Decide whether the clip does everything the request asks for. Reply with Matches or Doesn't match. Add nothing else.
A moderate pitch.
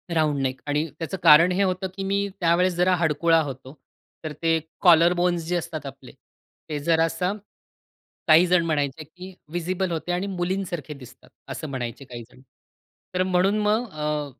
Matches